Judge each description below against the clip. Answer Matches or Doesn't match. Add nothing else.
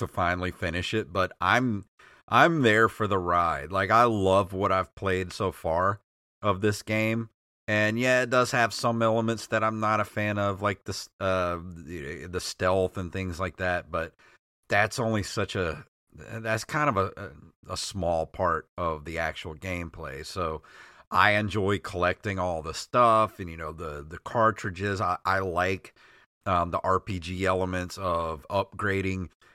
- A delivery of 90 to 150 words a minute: Doesn't match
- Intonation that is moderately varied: Matches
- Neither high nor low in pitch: Doesn't match